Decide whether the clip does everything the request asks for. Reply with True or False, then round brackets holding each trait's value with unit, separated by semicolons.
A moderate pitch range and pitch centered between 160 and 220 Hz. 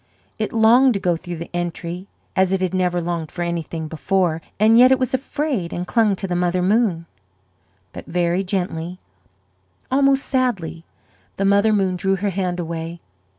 True (3.8 semitones; 185 Hz)